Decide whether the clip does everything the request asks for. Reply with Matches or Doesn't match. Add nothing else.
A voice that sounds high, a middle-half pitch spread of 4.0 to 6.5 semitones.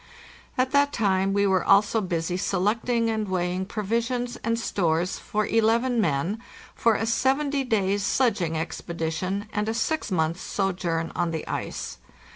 Matches